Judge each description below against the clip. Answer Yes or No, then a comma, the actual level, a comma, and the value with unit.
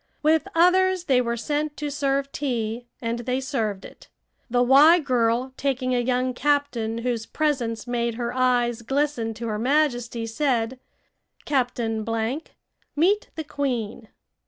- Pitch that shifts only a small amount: No, average, 3.7 semitones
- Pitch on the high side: Yes, very high, 250 Hz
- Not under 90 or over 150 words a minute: Yes, average, 140 wpm